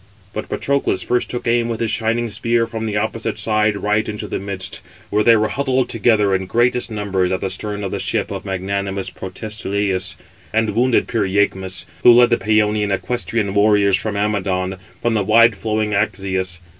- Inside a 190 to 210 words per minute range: No, average, 180 wpm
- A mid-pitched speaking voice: No, low, 105 Hz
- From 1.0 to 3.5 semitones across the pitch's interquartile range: Yes, narrow, 2.6 semitones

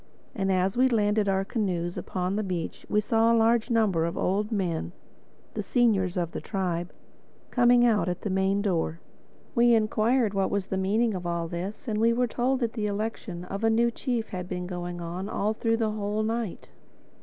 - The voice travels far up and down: No, average, 3.8 semitones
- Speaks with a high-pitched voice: Yes, high, 205 Hz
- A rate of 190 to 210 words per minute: Yes, average, 195 wpm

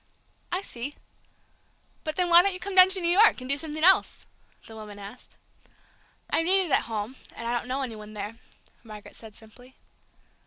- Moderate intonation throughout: No, wide, 8.1 semitones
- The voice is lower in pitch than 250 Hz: No, very high, 260 Hz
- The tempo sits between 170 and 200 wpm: Yes, average, 195 wpm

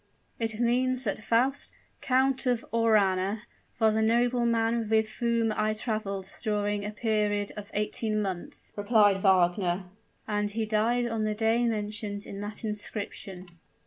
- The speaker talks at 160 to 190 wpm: No, average, 140 wpm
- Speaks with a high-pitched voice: Yes, high, 215 Hz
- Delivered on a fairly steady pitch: Yes, narrow, 2.0 semitones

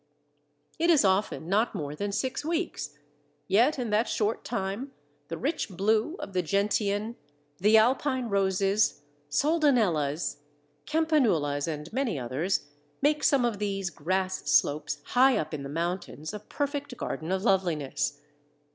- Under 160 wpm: Yes, average, 140 wpm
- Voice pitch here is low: No, high, 200 Hz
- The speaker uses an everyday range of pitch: No, wide, 7.2 semitones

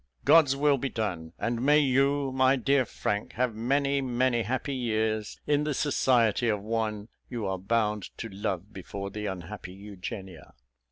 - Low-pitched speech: Yes, low, 115 Hz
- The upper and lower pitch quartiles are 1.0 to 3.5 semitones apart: No, average, 4.3 semitones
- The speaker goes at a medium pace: Yes, average, 160 wpm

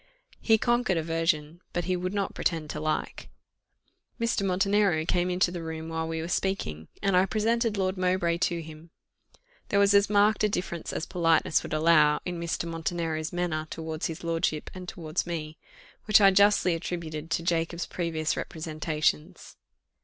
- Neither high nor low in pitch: Yes, medium, 170 Hz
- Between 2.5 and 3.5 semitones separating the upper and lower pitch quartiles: Yes, average, 2.8 semitones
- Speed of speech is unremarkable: Yes, average, 165 wpm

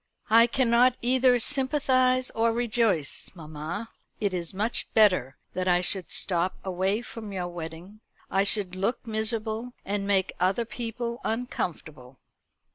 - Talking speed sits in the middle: No, slow, 130 wpm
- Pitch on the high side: Yes, high, 210 Hz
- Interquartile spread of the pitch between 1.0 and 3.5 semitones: No, average, 4.6 semitones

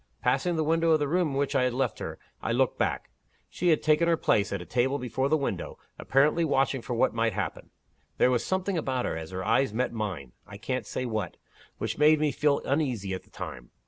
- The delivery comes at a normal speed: No, fast, 235 wpm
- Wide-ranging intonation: Yes, wide, 5.7 semitones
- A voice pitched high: No, low, 130 Hz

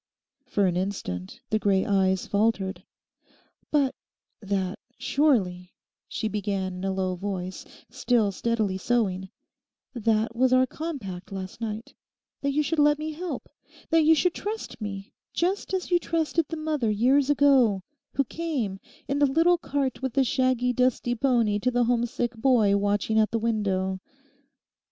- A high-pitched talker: Yes, high, 230 Hz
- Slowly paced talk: No, average, 150 wpm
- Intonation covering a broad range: Yes, wide, 6.0 semitones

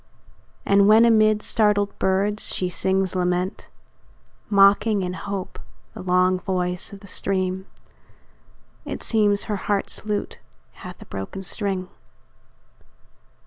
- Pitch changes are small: Yes, narrow, 2.0 semitones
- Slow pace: Yes, slow, 115 wpm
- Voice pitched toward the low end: No, high, 195 Hz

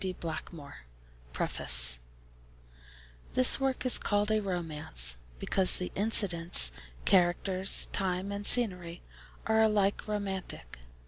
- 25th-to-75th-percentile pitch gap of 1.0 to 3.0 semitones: No, average, 3.8 semitones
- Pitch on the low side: No, medium, 185 Hz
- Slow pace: Yes, slow, 105 wpm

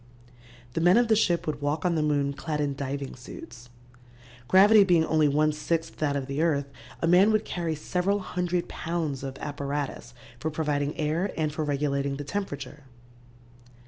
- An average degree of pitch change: Yes, average, 3.4 semitones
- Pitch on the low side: No, medium, 150 Hz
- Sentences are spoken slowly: No, average, 175 wpm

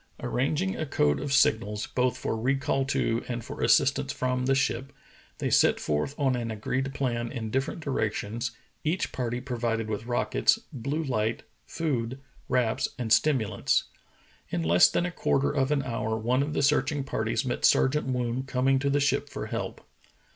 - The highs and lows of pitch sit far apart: No, average, 3.2 semitones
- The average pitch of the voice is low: Yes, low, 130 Hz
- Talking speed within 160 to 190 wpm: Yes, average, 170 wpm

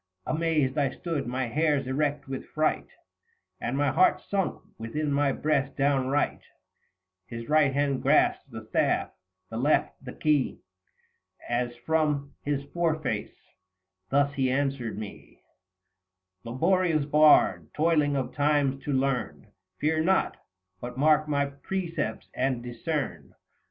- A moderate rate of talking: No, slow, 130 wpm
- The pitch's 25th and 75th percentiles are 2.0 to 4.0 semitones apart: Yes, average, 2.8 semitones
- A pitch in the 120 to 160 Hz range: Yes, medium, 140 Hz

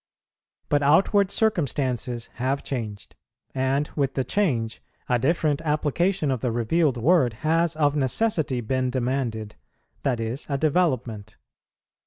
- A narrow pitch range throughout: No, average, 4.4 semitones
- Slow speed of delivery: Yes, slow, 125 wpm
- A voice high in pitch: No, low, 135 Hz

